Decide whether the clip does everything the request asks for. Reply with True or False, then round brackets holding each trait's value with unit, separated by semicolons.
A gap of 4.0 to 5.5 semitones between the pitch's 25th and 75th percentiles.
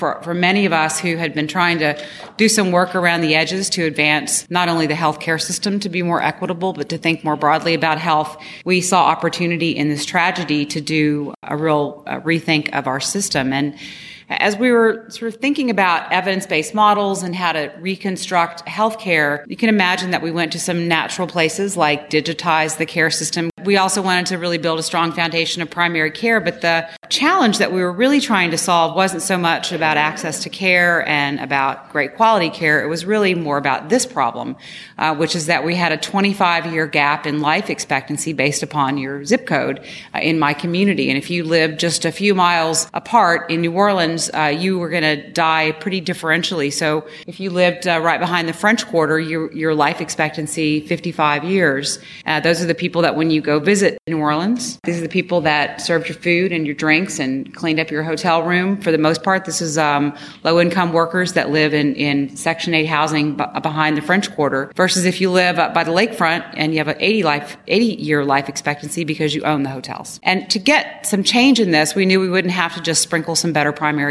False (2.9 semitones)